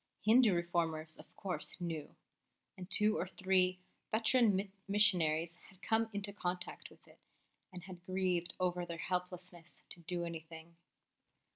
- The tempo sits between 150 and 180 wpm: No, slow, 135 wpm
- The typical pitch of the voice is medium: Yes, medium, 180 Hz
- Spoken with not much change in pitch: Yes, narrow, 2.3 semitones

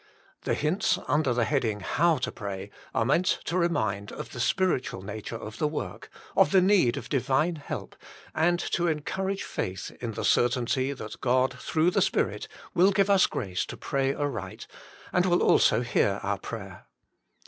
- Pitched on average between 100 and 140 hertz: Yes, low, 135 Hz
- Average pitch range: No, wide, 7.6 semitones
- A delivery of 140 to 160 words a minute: No, average, 170 wpm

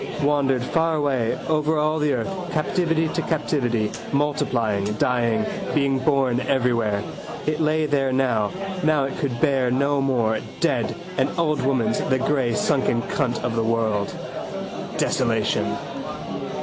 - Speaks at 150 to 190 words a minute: No, slow, 135 wpm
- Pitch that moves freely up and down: No, average, 4.2 semitones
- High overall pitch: No, low, 135 Hz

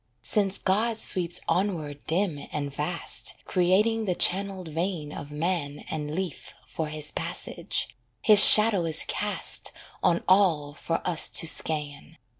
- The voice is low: No, medium, 175 Hz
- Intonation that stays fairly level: No, average, 4.3 semitones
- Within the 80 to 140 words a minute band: Yes, slow, 135 wpm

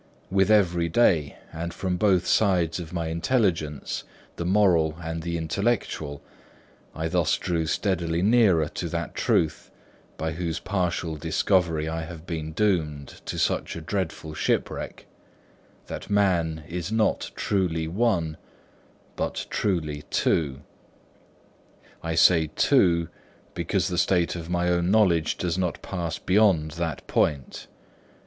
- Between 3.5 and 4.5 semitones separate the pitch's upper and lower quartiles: No, narrow, 2.6 semitones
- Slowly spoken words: Yes, slow, 130 wpm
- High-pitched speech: No, very low, 85 Hz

